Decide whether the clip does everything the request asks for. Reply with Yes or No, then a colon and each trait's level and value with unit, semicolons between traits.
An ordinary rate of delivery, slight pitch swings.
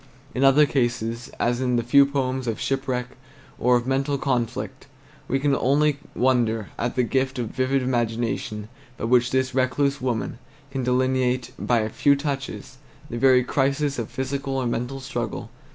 Yes: average, 165 wpm; narrow, 2.0 semitones